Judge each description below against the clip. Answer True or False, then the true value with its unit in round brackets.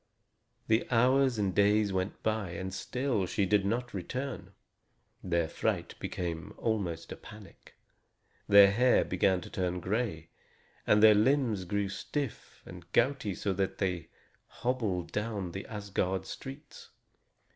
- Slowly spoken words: True (130 wpm)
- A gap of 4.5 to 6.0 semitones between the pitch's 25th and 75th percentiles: False (3.8 semitones)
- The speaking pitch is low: True (100 Hz)